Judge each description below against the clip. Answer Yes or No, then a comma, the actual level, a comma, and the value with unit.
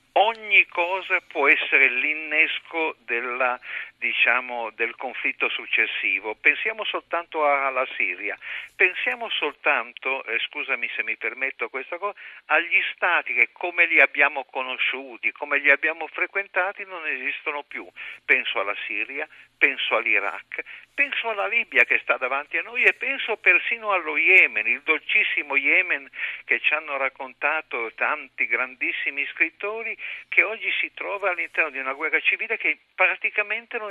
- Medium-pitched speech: Yes, medium, 160 Hz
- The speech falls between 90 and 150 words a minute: Yes, average, 135 wpm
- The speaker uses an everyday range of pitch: No, wide, 6.2 semitones